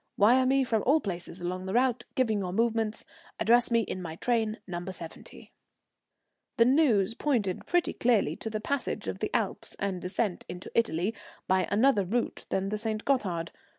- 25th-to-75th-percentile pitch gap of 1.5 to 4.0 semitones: No, average, 4.4 semitones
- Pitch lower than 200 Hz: No, high, 215 Hz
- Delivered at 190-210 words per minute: No, average, 175 wpm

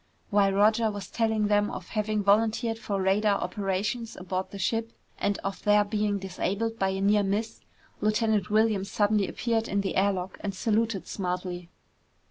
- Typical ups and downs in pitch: No, narrow, 2.0 semitones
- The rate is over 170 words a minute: No, average, 165 wpm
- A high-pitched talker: Yes, high, 205 Hz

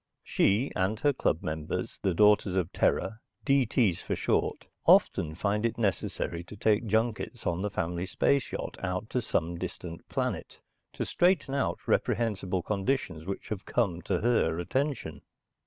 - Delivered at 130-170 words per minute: Yes, average, 155 wpm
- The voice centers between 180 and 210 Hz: No, low, 100 Hz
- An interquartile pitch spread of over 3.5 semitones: Yes, average, 5.0 semitones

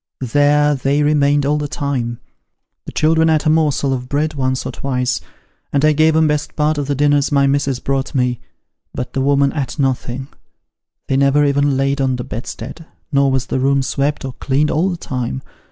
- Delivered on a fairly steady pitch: Yes, narrow, 1.9 semitones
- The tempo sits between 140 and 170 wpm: No, average, 195 wpm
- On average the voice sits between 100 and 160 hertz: Yes, medium, 140 Hz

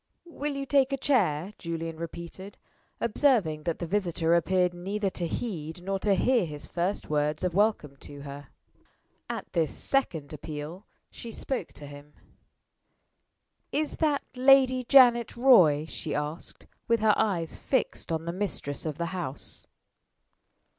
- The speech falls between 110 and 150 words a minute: Yes, average, 145 wpm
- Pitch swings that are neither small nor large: No, wide, 6.9 semitones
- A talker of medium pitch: Yes, medium, 180 Hz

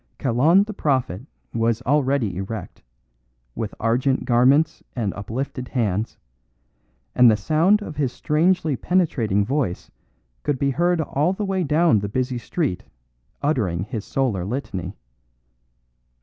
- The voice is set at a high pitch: No, low, 130 Hz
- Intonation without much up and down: No, wide, 5.6 semitones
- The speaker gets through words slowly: Yes, slow, 125 wpm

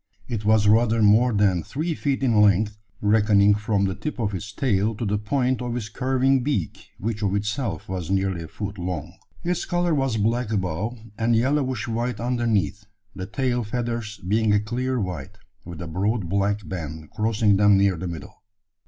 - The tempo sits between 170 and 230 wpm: Yes, average, 180 wpm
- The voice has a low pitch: Yes, low, 105 Hz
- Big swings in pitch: No, average, 3.5 semitones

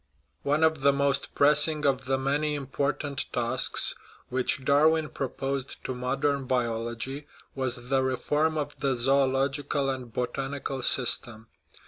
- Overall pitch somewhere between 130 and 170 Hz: Yes, low, 135 Hz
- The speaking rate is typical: No, slow, 125 wpm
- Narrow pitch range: Yes, narrow, 1.8 semitones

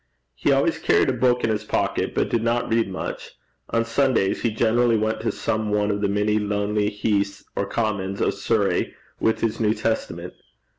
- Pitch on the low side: Yes, low, 110 Hz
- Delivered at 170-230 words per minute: Yes, average, 190 wpm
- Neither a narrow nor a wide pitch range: No, narrow, 2.0 semitones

